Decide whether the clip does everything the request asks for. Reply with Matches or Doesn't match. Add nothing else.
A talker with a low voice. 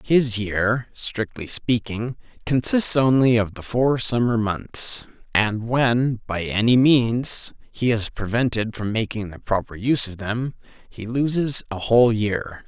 Matches